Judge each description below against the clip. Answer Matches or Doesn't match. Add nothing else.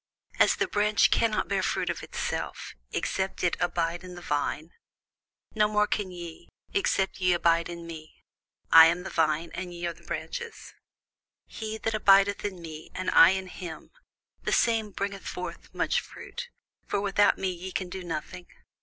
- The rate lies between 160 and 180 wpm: Matches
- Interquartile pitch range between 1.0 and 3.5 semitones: Matches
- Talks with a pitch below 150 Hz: Doesn't match